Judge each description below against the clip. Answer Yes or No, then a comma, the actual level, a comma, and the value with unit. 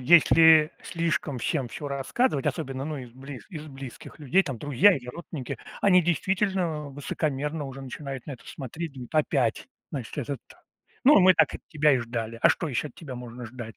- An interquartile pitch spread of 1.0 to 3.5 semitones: No, average, 3.9 semitones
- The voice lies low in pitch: No, medium, 145 Hz